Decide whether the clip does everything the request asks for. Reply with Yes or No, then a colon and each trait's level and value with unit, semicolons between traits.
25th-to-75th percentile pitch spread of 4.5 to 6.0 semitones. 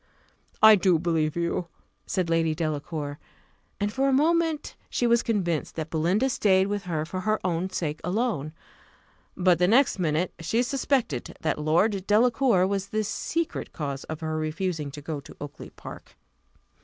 Yes: wide, 5.4 semitones